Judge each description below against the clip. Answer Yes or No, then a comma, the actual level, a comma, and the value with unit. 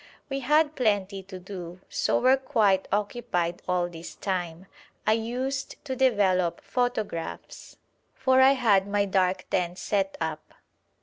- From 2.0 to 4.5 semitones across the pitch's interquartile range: No, wide, 5.4 semitones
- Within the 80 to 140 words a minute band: Yes, slow, 135 wpm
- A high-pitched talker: Yes, high, 200 Hz